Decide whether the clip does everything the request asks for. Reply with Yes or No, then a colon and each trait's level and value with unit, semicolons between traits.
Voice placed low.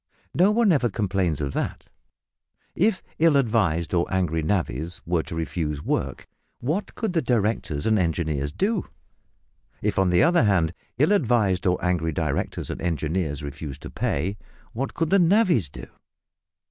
Yes: very low, 95 Hz